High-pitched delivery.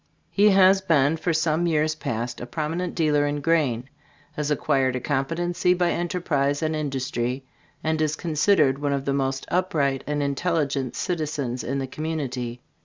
No: medium, 150 Hz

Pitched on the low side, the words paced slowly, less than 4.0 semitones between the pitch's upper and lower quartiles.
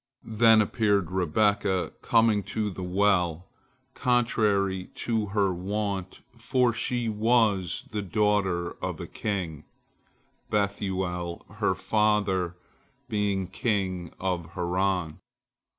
Yes: low, 100 Hz; slow, 100 wpm; average, 2.8 semitones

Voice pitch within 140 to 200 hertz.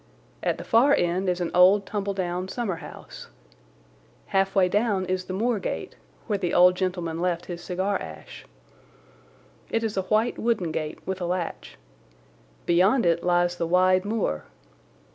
Yes: medium, 185 Hz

